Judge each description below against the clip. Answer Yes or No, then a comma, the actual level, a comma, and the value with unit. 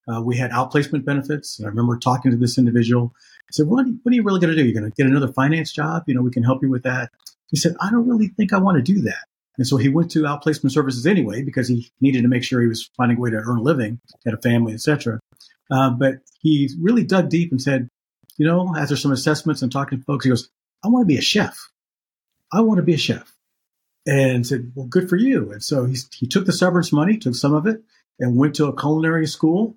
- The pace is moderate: No, fast, 265 wpm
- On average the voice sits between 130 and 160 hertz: Yes, medium, 140 Hz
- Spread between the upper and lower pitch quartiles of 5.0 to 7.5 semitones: No, average, 4.6 semitones